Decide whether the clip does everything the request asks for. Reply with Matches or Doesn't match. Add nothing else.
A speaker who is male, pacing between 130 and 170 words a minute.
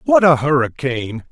Matches